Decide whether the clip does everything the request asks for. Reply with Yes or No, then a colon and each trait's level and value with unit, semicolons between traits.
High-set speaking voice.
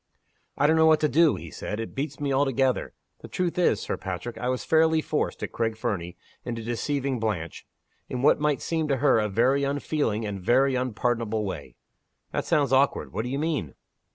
No: low, 130 Hz